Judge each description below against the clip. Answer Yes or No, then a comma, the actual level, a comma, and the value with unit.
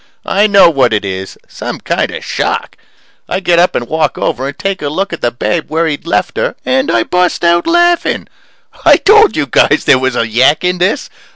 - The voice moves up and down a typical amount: No, wide, 7.0 semitones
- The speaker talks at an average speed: No, fast, 215 wpm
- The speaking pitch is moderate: Yes, medium, 170 Hz